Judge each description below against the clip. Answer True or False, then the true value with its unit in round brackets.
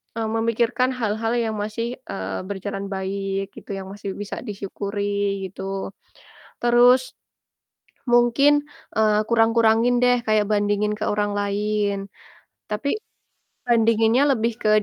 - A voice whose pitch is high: True (215 Hz)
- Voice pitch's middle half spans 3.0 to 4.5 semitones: False (2.5 semitones)